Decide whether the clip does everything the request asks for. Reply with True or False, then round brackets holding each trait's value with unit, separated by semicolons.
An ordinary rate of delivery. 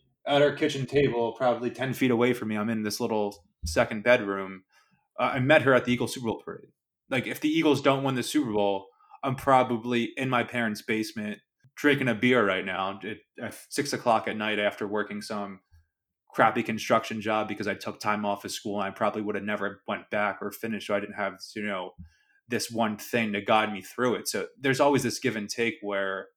False (220 wpm)